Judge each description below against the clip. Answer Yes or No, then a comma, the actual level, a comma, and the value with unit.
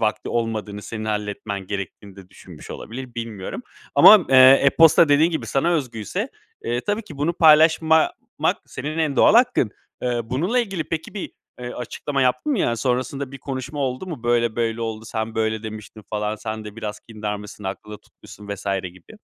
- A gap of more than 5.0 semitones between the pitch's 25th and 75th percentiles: Yes, wide, 5.5 semitones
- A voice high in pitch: No, low, 120 Hz